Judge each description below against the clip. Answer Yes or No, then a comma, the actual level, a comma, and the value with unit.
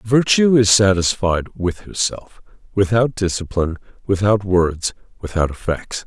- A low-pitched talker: Yes, low, 100 Hz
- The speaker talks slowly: Yes, slow, 110 wpm